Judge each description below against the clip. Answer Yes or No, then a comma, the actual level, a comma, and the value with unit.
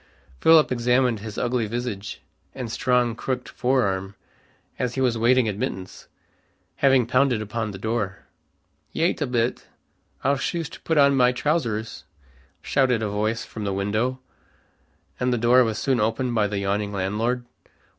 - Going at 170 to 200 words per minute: No, average, 150 wpm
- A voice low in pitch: Yes, low, 120 Hz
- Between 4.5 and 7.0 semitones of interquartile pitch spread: No, average, 3.2 semitones